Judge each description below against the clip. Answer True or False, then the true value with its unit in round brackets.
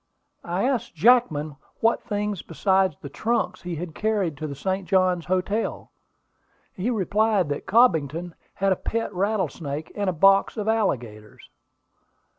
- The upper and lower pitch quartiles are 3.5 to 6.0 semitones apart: True (4.8 semitones)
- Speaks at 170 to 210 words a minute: False (140 wpm)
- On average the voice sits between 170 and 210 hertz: True (190 Hz)